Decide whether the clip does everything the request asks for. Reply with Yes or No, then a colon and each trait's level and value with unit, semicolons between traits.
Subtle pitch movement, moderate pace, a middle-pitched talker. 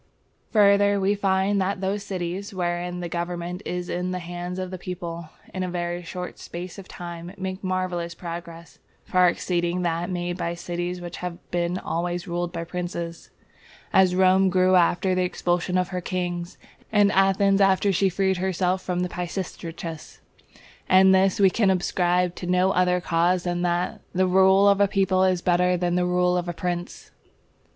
Yes: narrow, 1.3 semitones; average, 175 wpm; medium, 180 Hz